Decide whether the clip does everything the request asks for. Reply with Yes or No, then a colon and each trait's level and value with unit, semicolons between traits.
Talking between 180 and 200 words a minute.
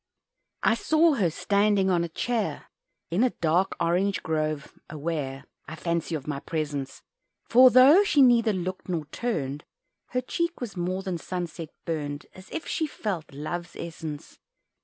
No: average, 155 wpm